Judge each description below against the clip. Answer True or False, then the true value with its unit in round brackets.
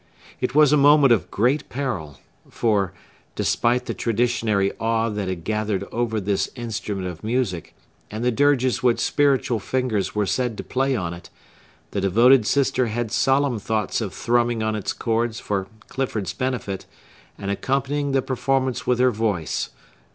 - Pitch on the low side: True (115 Hz)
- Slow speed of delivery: False (150 wpm)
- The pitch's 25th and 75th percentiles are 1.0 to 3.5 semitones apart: False (3.9 semitones)